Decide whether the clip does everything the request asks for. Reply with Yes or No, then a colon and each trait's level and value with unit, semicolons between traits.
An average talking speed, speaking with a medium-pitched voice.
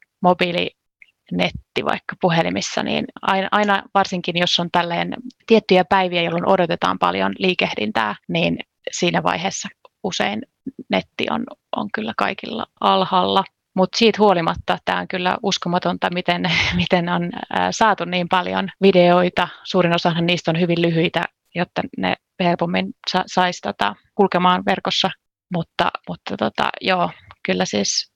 Yes: average, 130 wpm; medium, 180 Hz